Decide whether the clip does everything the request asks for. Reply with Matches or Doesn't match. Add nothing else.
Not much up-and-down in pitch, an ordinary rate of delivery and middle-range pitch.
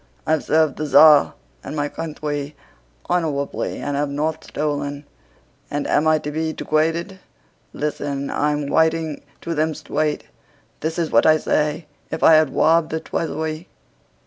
Matches